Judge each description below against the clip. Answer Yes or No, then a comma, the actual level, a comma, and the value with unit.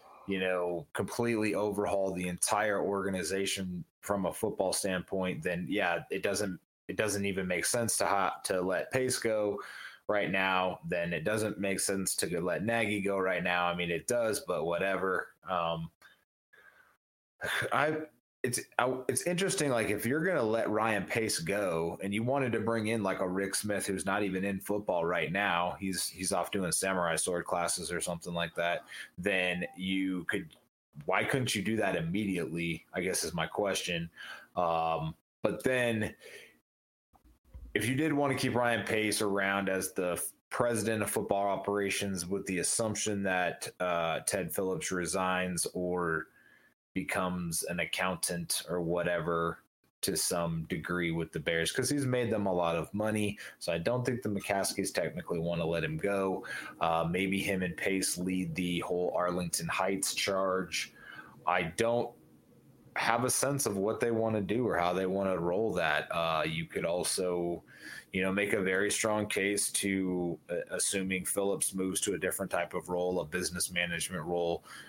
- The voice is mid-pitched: No, very low, 95 Hz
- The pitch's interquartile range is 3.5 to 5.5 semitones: No, average, 2.8 semitones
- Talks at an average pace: Yes, average, 170 wpm